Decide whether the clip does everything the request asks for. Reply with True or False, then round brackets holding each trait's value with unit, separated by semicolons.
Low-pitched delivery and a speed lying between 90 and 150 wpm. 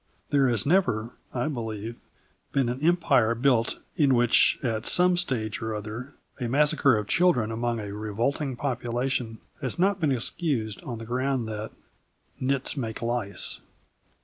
True (120 Hz; 145 wpm)